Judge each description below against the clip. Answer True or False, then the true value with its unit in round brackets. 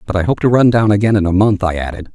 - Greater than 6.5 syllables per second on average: True (7.1 syllables/s)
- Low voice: True (100 Hz)